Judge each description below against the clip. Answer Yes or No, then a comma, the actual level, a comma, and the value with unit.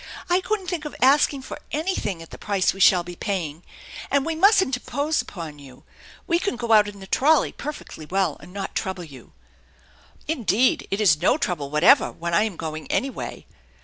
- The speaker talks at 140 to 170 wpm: No, average, 200 wpm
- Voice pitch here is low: No, high, 200 Hz